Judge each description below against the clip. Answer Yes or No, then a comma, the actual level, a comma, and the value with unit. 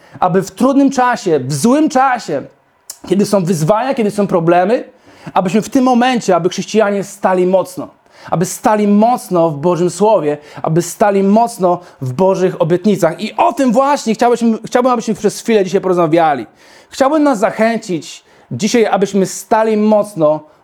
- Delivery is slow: No, average, 150 wpm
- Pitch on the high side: Yes, high, 205 Hz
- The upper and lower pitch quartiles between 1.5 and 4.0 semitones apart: No, average, 4.6 semitones